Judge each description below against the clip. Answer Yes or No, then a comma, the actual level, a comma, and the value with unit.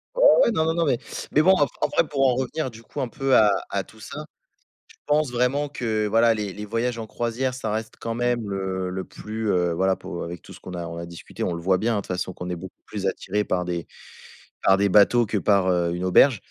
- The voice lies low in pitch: Yes, low, 110 Hz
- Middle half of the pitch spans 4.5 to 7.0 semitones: Yes, average, 4.9 semitones